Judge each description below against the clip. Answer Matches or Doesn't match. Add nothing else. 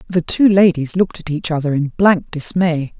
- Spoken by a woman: Matches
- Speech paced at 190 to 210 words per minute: Matches